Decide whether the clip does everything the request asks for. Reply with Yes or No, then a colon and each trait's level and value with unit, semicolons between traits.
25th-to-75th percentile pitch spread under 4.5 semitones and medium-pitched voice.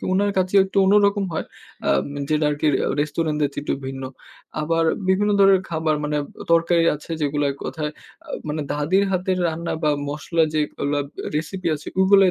Yes: average, 4.0 semitones; medium, 160 Hz